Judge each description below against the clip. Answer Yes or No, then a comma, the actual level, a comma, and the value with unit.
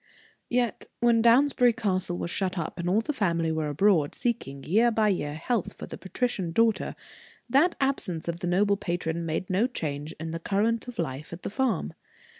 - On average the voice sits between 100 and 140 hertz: No, high, 190 Hz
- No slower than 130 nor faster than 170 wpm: No, average, 190 wpm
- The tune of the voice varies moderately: No, wide, 5.9 semitones